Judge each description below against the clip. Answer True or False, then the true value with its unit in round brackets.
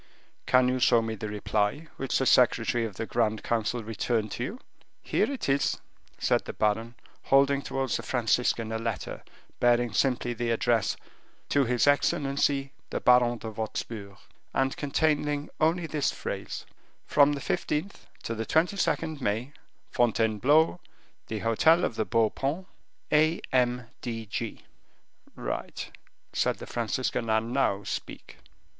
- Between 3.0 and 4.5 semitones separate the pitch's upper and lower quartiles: True (3.9 semitones)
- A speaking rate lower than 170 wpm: True (145 wpm)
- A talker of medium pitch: False (120 Hz)